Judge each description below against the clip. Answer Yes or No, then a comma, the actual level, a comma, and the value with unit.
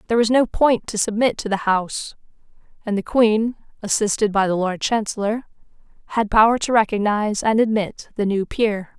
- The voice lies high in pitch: Yes, high, 215 Hz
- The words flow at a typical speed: Yes, average, 175 wpm